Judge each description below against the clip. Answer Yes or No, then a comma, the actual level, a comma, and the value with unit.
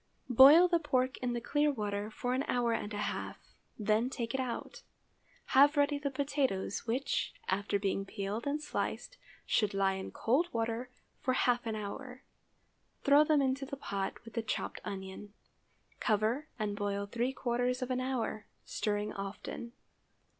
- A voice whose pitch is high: Yes, high, 240 Hz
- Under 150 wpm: No, average, 160 wpm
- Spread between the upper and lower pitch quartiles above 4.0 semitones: Yes, average, 4.5 semitones